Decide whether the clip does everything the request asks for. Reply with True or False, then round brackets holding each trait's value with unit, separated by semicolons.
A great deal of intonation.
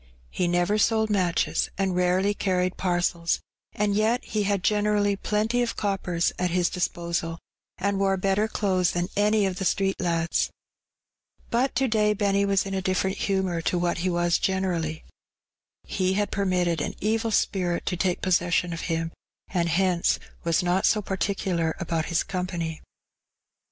False (2.5 semitones)